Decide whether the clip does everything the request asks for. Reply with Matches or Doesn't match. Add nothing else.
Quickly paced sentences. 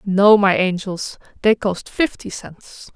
Doesn't match